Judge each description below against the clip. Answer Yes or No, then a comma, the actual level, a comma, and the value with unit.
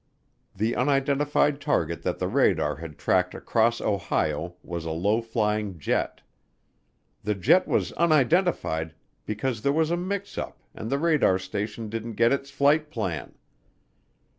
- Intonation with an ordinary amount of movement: No, wide, 7.4 semitones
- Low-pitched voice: Yes, low, 115 Hz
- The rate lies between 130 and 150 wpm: Yes, average, 140 wpm